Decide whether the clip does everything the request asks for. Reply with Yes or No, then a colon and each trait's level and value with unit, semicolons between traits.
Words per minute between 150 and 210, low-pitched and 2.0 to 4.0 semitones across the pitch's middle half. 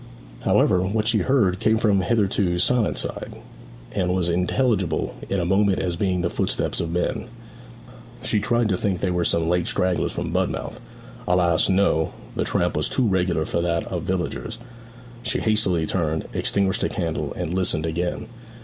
Yes: average, 170 wpm; very low, 90 Hz; average, 3.1 semitones